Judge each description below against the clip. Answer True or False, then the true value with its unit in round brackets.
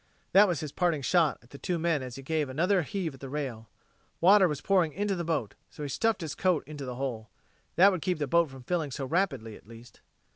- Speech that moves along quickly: True (245 wpm)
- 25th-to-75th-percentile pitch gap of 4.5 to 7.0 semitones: True (4.9 semitones)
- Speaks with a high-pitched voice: False (155 Hz)